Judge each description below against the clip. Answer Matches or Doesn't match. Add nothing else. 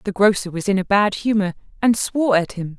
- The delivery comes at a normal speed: Doesn't match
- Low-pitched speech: Doesn't match